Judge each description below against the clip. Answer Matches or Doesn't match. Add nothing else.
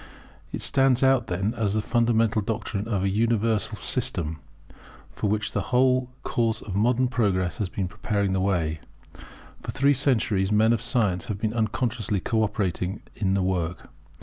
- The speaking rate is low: Doesn't match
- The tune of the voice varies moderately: Matches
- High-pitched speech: Doesn't match